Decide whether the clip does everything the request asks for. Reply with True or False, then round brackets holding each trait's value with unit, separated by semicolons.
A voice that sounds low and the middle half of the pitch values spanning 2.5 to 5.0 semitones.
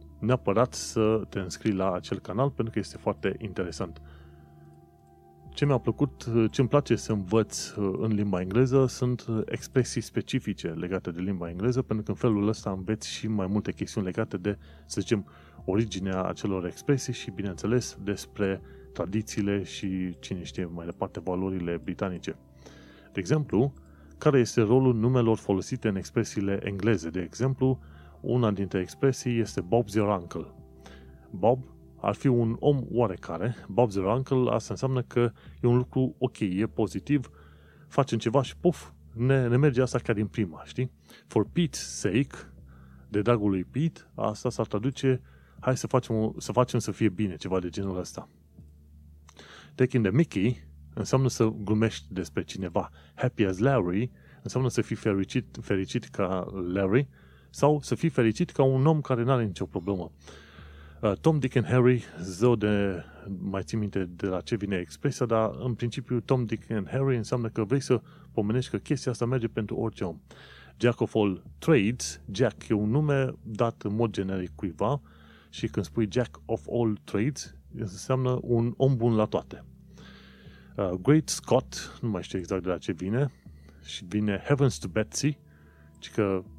False (105 Hz; 5.4 semitones)